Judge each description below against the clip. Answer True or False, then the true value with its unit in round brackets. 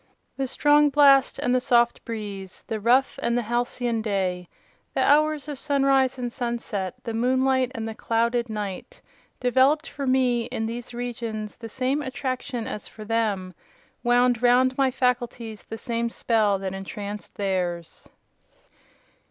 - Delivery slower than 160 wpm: True (145 wpm)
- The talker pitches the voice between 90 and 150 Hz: False (240 Hz)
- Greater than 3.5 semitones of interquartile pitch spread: False (3.1 semitones)